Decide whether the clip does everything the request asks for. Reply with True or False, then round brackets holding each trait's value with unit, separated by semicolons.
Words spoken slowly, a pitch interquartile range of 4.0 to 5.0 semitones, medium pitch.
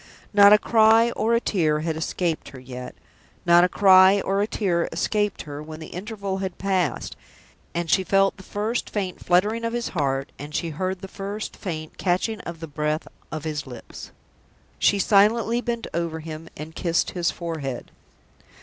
False (175 wpm; 4.4 semitones; 180 Hz)